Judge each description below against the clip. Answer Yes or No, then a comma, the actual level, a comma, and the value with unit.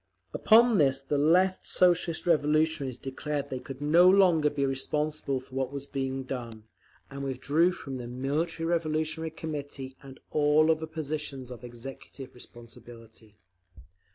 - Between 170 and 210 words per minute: No, slow, 135 wpm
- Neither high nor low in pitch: Yes, medium, 145 Hz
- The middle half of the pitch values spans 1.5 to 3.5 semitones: Yes, average, 3.1 semitones